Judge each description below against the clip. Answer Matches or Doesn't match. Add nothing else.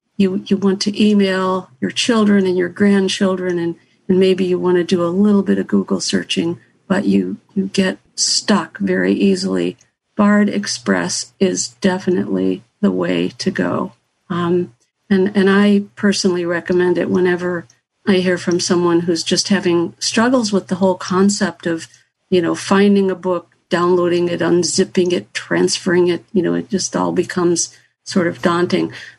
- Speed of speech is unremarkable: Matches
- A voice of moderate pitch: Matches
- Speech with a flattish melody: Matches